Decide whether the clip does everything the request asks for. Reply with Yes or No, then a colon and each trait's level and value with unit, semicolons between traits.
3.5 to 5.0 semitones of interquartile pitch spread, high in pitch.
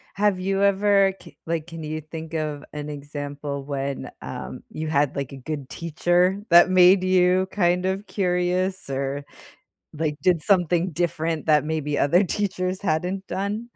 No: average, 3.8 semitones; medium, 170 Hz